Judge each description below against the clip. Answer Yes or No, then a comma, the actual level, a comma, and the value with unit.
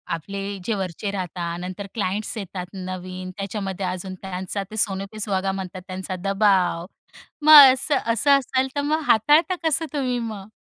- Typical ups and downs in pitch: Yes, average, 3.3 semitones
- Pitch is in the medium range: No, high, 195 Hz